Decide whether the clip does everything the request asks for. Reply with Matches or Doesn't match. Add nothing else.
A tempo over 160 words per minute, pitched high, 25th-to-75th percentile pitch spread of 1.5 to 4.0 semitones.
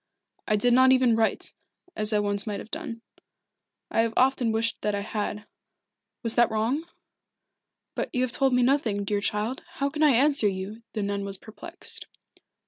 Matches